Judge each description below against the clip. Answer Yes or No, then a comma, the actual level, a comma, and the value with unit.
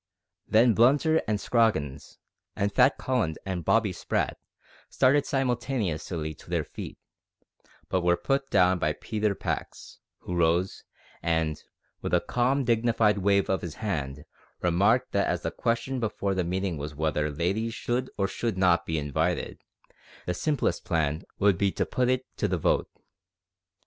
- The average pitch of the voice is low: Yes, low, 100 Hz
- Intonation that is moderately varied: No, wide, 5.8 semitones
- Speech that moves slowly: No, average, 160 wpm